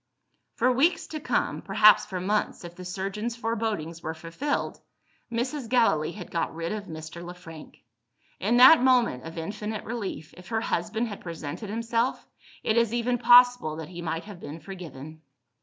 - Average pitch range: No, wide, 5.9 semitones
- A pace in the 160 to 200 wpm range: Yes, average, 170 wpm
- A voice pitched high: Yes, high, 205 Hz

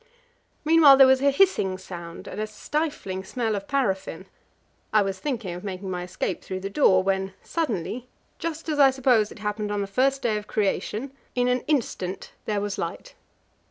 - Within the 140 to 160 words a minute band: No, average, 185 wpm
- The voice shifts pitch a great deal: Yes, wide, 5.9 semitones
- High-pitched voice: Yes, high, 215 Hz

